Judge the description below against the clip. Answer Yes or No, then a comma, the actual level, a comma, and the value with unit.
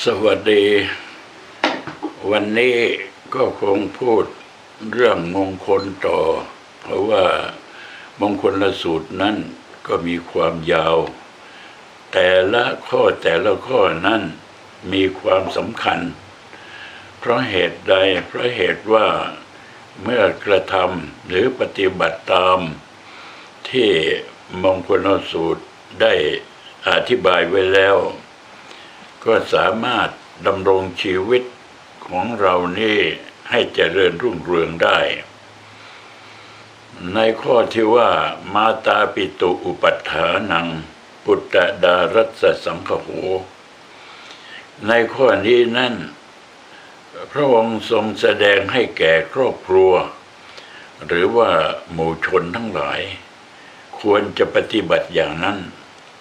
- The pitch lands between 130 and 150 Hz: No, low, 115 Hz